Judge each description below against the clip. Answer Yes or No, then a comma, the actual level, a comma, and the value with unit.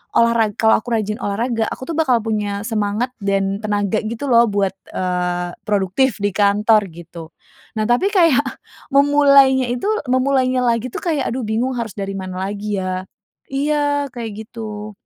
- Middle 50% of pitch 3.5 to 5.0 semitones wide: Yes, average, 4.1 semitones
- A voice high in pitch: Yes, high, 220 Hz